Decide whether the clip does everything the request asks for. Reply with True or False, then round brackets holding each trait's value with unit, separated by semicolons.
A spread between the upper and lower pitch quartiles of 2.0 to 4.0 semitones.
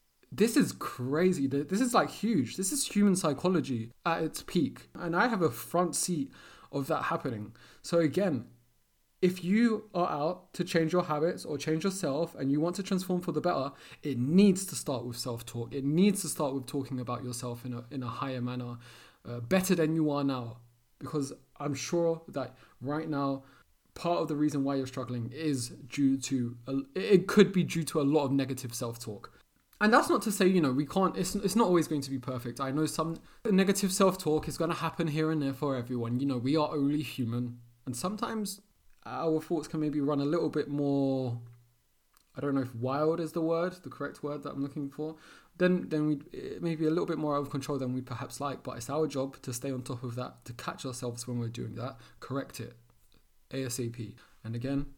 False (4.8 semitones)